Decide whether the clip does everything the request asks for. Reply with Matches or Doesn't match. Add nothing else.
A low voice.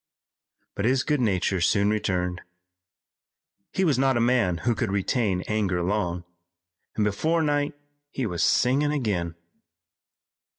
Matches